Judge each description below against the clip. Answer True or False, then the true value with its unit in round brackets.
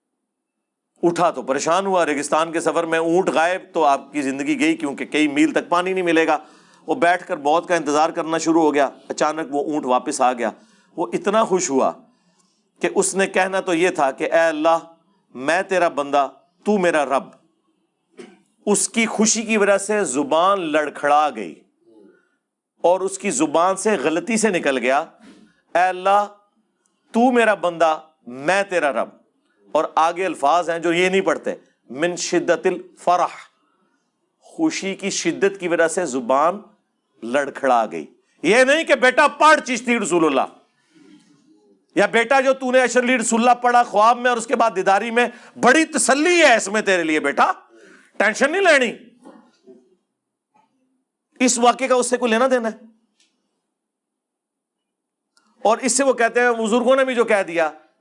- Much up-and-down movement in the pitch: True (6.7 semitones)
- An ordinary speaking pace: True (170 wpm)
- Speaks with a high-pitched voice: True (195 Hz)